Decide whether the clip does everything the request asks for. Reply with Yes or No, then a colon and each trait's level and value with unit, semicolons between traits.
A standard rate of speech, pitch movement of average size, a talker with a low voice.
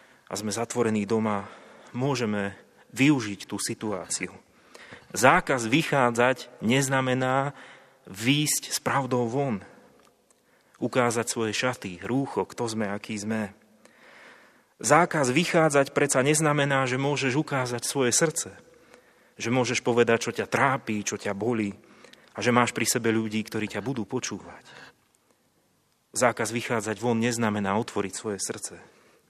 Yes: average, 120 wpm; average, 3.7 semitones; low, 120 Hz